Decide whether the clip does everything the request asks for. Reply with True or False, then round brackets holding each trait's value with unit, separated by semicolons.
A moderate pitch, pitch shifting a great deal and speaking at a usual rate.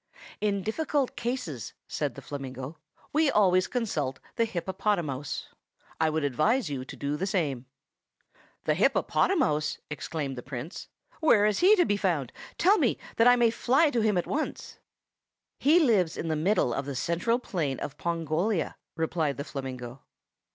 True (170 Hz; 8.2 semitones; 160 wpm)